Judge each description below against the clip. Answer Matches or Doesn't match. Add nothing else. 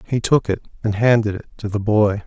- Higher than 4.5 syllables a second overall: Matches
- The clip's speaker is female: Doesn't match